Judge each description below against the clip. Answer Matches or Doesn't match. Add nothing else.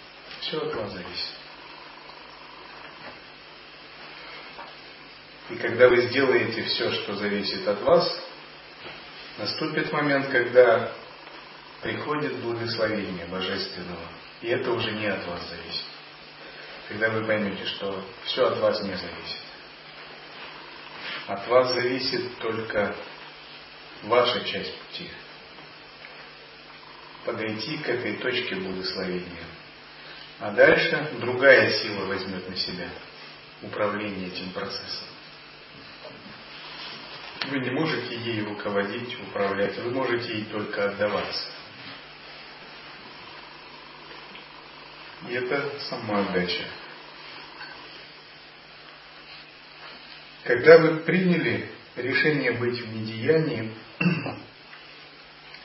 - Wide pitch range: Doesn't match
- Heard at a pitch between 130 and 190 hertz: Doesn't match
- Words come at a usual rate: Doesn't match